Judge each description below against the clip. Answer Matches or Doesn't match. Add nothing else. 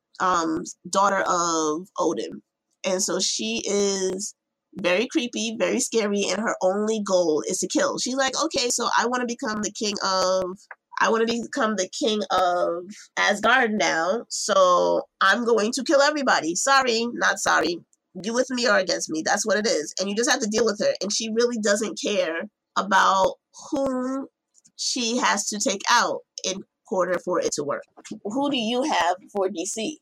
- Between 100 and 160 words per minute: Doesn't match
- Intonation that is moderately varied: Doesn't match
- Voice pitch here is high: Matches